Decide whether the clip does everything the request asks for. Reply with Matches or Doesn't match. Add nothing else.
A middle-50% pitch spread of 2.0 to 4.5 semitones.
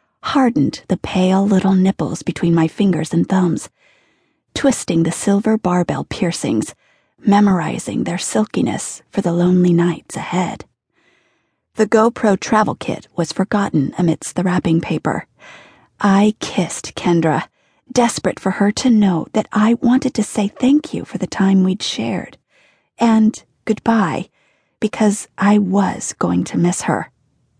Matches